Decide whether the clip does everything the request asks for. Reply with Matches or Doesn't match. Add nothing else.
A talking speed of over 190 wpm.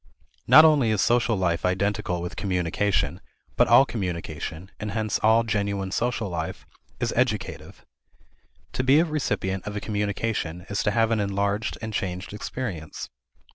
Doesn't match